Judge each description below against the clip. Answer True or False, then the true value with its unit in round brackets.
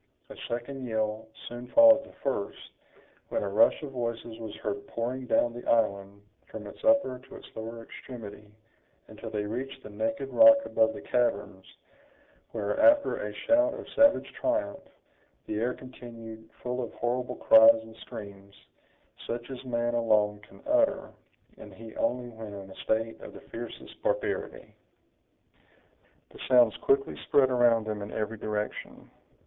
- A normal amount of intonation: True (3.4 semitones)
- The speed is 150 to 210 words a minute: True (155 wpm)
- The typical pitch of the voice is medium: False (115 Hz)